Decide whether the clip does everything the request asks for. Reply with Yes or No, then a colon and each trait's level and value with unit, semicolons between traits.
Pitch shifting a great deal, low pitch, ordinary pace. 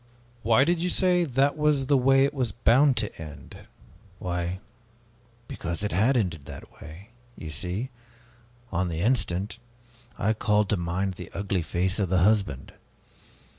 Yes: wide, 6.9 semitones; low, 100 Hz; average, 160 wpm